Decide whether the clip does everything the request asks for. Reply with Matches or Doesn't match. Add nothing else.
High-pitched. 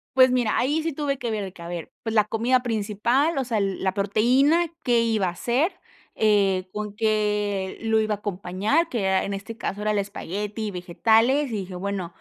Matches